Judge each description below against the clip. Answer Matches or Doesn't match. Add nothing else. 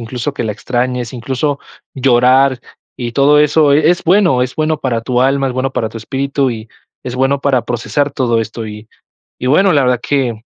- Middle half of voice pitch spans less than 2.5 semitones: Doesn't match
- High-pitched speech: Doesn't match